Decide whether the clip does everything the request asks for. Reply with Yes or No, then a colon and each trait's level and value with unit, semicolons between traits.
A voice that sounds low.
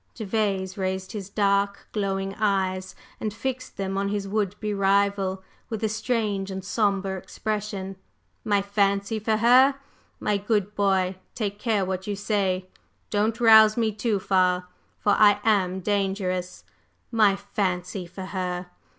No: high, 200 Hz